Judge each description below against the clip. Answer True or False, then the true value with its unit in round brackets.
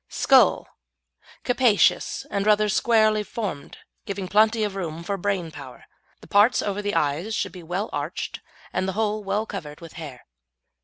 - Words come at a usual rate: True (160 wpm)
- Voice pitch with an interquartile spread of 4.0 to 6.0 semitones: False (3.5 semitones)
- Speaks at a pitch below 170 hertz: False (200 Hz)